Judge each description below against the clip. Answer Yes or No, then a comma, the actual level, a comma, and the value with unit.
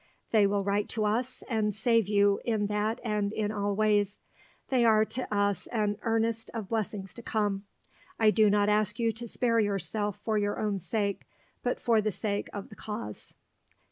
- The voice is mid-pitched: No, high, 210 Hz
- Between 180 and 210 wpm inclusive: Yes, average, 185 wpm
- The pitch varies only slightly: Yes, narrow, 1.7 semitones